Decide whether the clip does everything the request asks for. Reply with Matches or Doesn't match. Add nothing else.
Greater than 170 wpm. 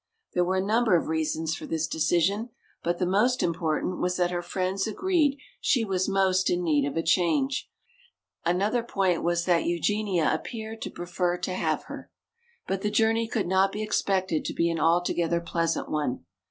Matches